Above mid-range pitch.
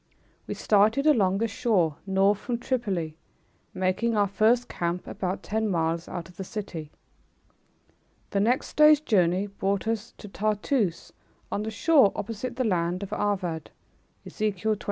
Yes: high, 205 Hz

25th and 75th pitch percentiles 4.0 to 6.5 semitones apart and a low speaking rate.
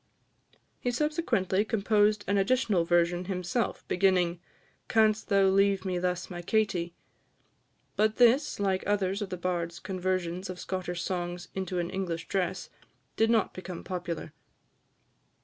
No: average, 2.7 semitones; slow, 130 wpm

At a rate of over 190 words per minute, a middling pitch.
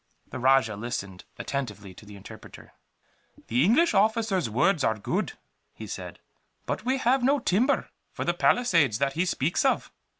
No: average, 160 wpm; medium, 160 Hz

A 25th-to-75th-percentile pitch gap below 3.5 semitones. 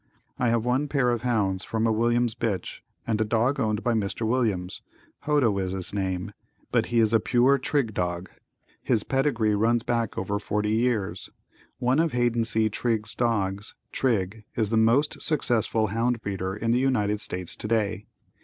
Yes: average, 2.7 semitones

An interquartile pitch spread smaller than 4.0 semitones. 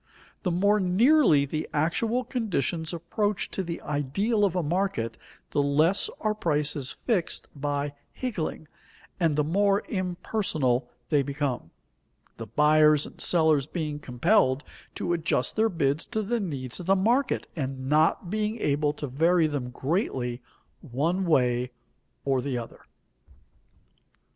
No: wide, 5.5 semitones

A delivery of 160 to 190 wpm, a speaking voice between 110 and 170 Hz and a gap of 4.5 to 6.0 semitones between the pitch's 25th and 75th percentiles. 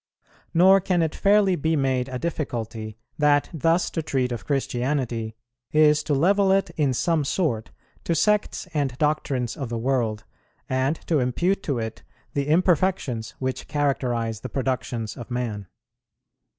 No: average, 150 wpm; medium, 140 Hz; average, 5.1 semitones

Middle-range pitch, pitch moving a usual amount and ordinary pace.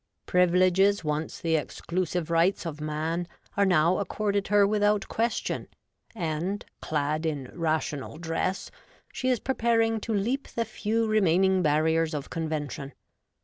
No: medium, 180 Hz; average, 4.6 semitones; slow, 130 wpm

